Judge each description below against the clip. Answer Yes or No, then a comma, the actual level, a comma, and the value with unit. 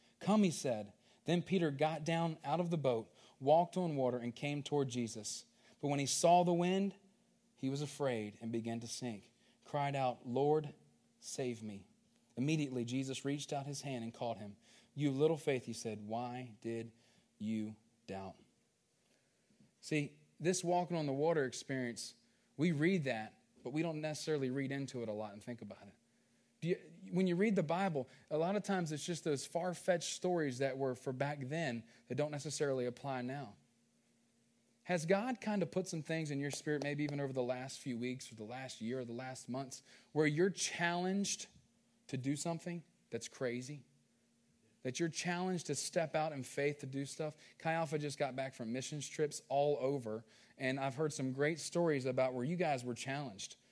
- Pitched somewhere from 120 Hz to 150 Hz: Yes, medium, 140 Hz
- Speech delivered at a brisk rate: No, average, 190 wpm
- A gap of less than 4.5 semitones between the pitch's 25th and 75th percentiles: No, average, 4.8 semitones